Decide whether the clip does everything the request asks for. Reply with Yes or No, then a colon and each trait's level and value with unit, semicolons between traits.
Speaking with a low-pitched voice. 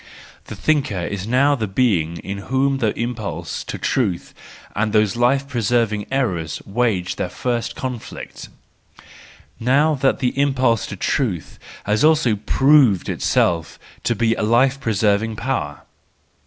Yes: low, 115 Hz